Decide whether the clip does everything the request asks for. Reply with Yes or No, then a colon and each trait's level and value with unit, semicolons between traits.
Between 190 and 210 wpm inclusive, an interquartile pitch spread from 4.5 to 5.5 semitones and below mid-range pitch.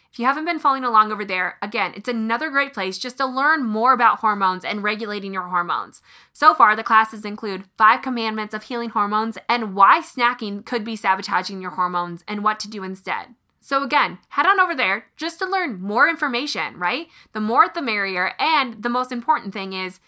No: fast, 205 wpm; average, 5.2 semitones; high, 220 Hz